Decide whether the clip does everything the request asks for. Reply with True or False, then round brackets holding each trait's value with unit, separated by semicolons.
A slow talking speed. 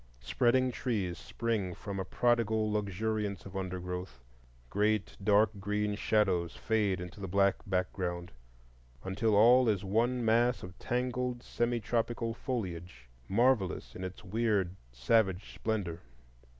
True (125 wpm)